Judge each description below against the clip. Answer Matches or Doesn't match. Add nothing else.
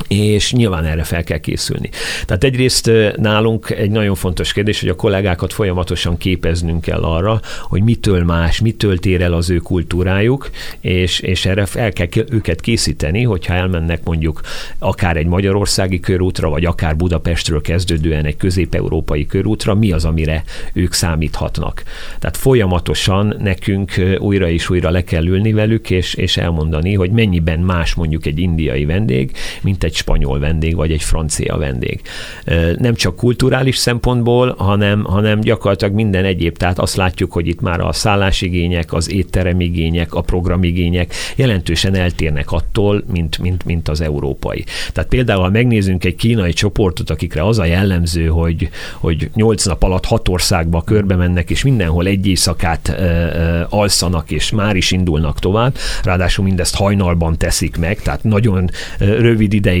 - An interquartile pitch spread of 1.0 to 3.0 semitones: Doesn't match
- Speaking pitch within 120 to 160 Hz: Doesn't match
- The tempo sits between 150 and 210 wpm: Matches